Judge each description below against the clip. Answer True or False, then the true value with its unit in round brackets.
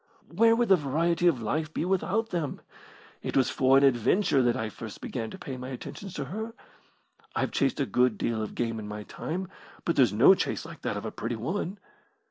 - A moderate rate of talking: False (215 wpm)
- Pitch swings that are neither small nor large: False (7.3 semitones)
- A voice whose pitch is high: False (140 Hz)